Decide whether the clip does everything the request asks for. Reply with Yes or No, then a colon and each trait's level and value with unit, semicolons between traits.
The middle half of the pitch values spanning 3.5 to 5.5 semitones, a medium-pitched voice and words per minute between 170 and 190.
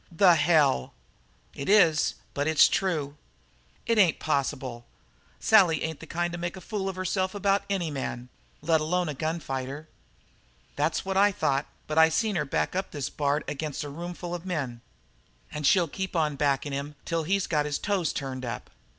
Yes: average, 4.2 semitones; medium, 160 Hz; average, 185 wpm